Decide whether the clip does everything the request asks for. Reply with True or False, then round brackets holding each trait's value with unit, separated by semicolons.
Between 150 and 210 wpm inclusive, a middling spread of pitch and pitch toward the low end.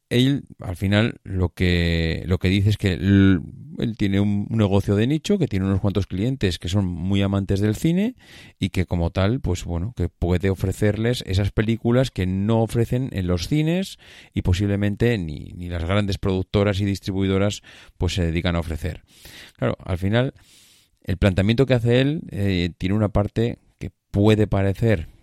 True (175 wpm; 3.2 semitones; 100 Hz)